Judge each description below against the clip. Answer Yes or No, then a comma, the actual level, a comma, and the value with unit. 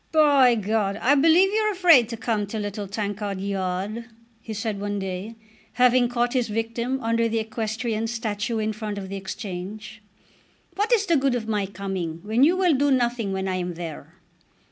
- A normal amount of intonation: Yes, average, 3.7 semitones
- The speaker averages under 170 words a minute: No, average, 185 wpm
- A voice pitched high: Yes, high, 220 Hz